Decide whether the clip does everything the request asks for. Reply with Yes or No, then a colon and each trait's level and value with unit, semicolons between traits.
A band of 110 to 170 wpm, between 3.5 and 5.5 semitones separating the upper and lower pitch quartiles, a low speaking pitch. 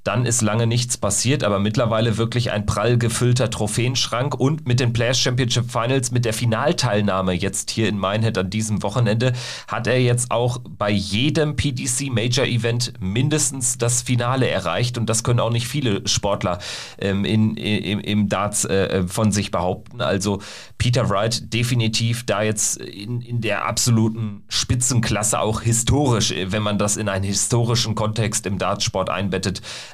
No: average, 160 wpm; average, 2.9 semitones; low, 115 Hz